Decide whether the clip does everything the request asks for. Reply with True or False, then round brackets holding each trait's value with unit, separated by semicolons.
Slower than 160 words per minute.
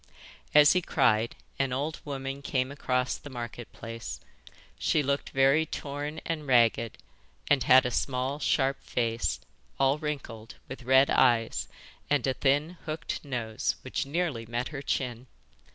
True (145 wpm)